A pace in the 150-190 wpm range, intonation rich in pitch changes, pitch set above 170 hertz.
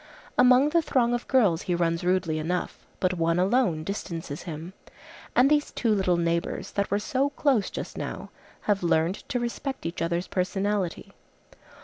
Yes: average, 160 wpm; wide, 6.1 semitones; high, 190 Hz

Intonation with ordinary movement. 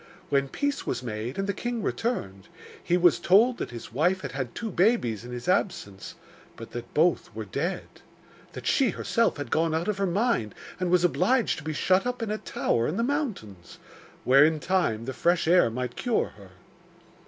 No: wide, 9.0 semitones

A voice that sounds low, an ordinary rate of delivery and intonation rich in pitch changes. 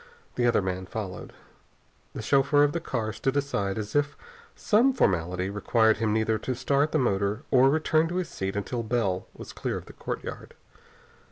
Yes: low, 115 Hz; average, 180 wpm; wide, 6.0 semitones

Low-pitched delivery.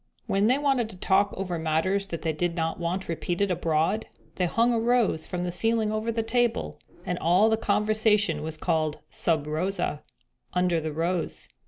No: medium, 185 Hz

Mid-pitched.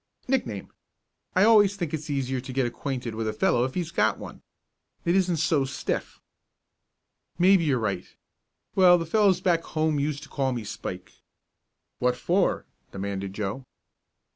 Yes: medium, 145 Hz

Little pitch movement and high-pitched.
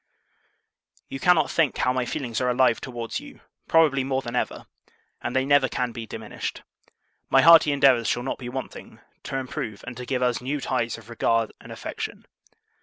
No: narrow, 2.1 semitones; low, 130 Hz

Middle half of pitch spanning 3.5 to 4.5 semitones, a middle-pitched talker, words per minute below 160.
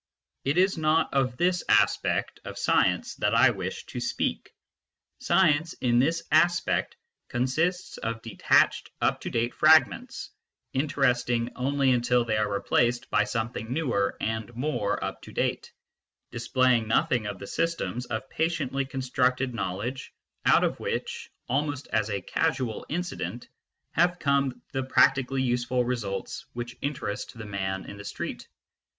No: average, 3.9 semitones; low, 125 Hz; average, 145 wpm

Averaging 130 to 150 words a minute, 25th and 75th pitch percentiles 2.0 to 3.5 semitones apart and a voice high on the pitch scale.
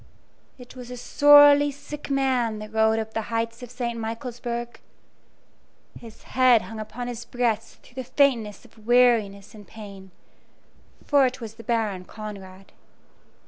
Yes: average, 145 wpm; narrow, 2.5 semitones; high, 230 Hz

